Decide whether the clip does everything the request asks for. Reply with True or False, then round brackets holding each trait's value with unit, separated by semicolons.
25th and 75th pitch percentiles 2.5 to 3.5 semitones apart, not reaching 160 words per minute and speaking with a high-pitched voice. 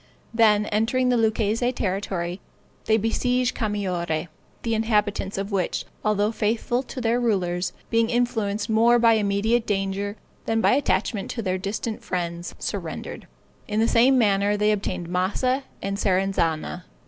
True (2.9 semitones; 140 wpm; 210 Hz)